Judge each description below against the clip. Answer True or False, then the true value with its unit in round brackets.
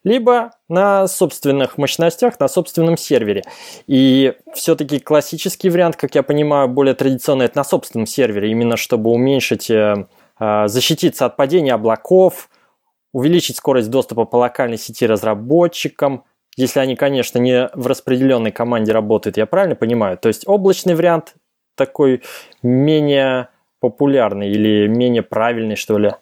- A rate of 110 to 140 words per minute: True (130 wpm)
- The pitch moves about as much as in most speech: False (5.8 semitones)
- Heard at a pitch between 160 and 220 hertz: False (135 Hz)